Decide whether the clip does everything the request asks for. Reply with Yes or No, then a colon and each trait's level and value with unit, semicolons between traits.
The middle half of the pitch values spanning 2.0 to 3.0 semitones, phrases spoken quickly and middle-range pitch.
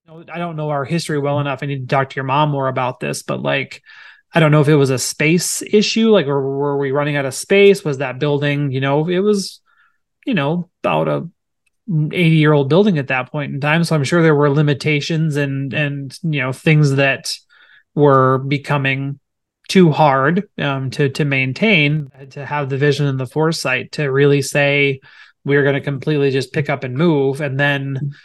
Yes: narrow, 2.5 semitones; fast, 210 wpm; medium, 145 Hz